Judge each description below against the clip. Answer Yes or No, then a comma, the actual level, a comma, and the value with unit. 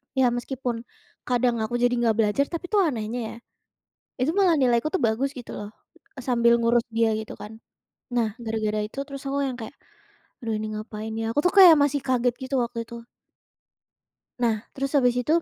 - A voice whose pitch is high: Yes, high, 240 Hz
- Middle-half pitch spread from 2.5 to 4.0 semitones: Yes, average, 3.4 semitones